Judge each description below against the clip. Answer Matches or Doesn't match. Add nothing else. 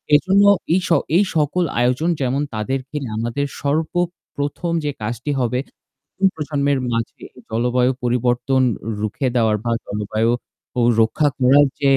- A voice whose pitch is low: Matches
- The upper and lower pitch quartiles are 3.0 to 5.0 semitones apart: Matches